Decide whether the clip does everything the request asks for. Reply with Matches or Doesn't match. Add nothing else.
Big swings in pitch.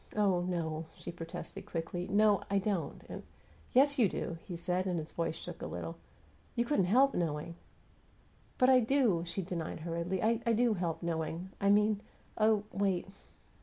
Doesn't match